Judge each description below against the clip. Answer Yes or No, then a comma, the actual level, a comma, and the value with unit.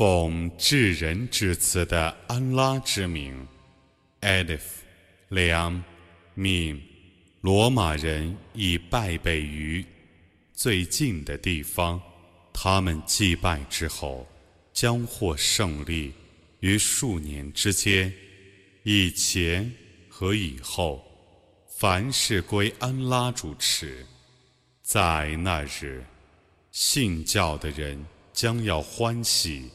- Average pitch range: Yes, average, 3.9 semitones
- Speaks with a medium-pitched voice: No, very low, 90 Hz